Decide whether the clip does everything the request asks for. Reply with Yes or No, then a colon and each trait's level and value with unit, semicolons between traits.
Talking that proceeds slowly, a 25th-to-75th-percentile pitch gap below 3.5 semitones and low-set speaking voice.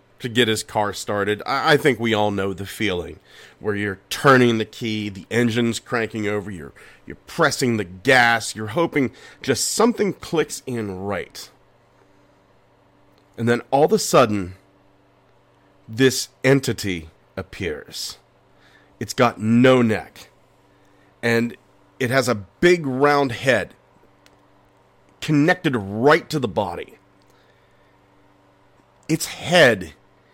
No: slow, 120 wpm; average, 4.9 semitones; low, 110 Hz